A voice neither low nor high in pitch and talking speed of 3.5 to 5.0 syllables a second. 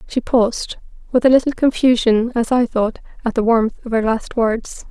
No: high, 235 Hz; 4.9 syllables/s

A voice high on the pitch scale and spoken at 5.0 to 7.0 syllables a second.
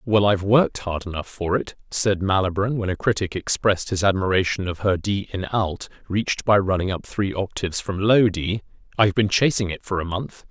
No: low, 100 Hz; 5.5 syllables/s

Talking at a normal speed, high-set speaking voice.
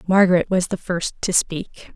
No: average, 185 wpm; medium, 180 Hz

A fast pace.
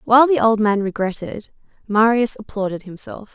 No: average, 145 wpm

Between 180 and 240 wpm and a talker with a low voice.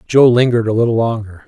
Yes: fast, 205 wpm; low, 115 Hz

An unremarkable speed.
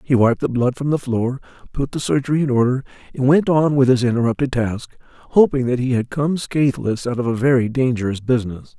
No: fast, 210 wpm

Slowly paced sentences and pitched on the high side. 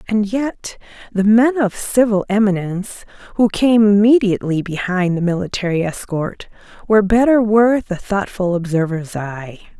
Yes: slow, 130 wpm; high, 200 Hz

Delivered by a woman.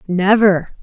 Yes: female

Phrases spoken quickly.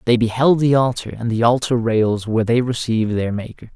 Yes: fast, 210 wpm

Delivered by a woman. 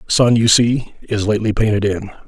No: male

